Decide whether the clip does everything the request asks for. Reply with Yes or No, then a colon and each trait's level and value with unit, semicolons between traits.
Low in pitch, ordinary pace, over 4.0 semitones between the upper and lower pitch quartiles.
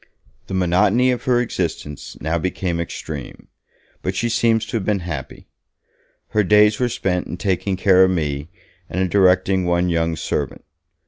No: very low, 95 Hz; average, 165 wpm; average, 3.5 semitones